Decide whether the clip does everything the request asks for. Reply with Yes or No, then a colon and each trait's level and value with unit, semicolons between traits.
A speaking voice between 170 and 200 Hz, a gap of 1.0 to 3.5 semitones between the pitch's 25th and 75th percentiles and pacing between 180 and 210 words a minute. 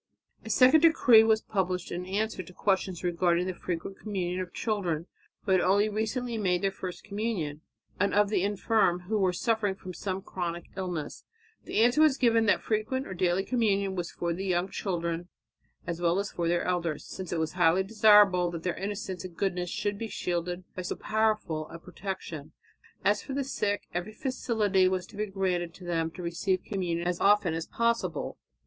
Yes: high, 190 Hz; average, 3.2 semitones; average, 185 wpm